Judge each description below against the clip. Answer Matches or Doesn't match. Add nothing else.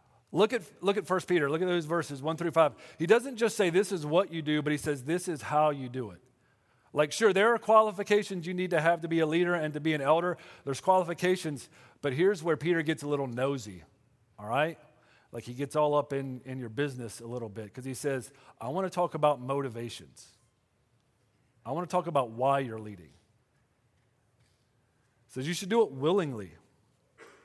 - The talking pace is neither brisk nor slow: Doesn't match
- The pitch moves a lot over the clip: Matches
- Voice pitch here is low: Doesn't match